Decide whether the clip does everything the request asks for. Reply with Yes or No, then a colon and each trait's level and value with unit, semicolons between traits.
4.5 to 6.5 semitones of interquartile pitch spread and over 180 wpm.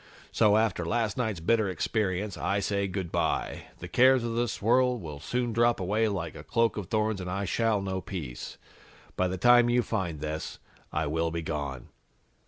Yes: average, 4.8 semitones; average, 190 wpm